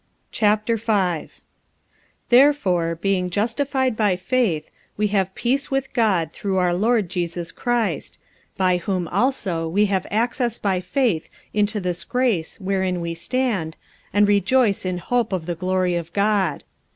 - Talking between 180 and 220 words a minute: No, average, 140 wpm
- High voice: Yes, high, 195 Hz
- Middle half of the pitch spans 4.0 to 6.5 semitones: Yes, average, 4.5 semitones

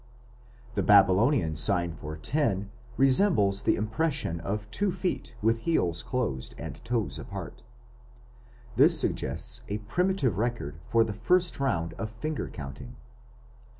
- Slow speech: Yes, slow, 125 wpm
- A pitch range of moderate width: No, wide, 7.2 semitones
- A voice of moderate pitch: No, low, 110 Hz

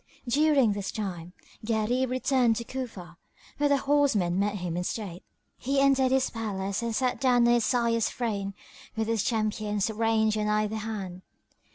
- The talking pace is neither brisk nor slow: Yes, average, 165 wpm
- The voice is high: Yes, high, 225 Hz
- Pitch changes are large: No, average, 3.6 semitones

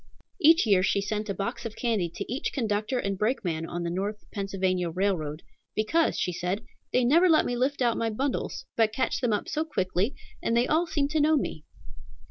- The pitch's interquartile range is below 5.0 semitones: No, wide, 5.6 semitones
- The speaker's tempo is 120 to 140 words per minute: No, fast, 205 wpm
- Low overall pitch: No, high, 215 Hz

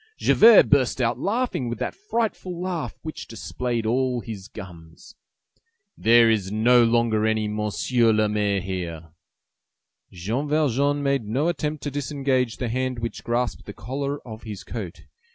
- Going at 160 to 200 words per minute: No, average, 150 wpm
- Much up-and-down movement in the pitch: No, average, 4.7 semitones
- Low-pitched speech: Yes, low, 120 Hz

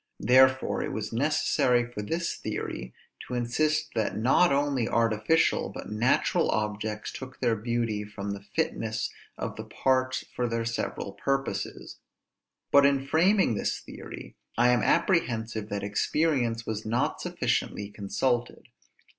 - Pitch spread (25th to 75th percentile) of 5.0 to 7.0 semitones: No, average, 3.8 semitones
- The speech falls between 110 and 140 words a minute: Yes, slow, 135 wpm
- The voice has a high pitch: No, low, 120 Hz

